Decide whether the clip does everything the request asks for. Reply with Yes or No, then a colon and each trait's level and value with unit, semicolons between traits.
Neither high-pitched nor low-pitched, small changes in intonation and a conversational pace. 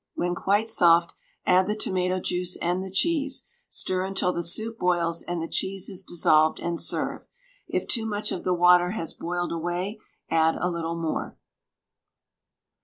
Yes: medium, 180 Hz; narrow, 2.1 semitones; average, 165 wpm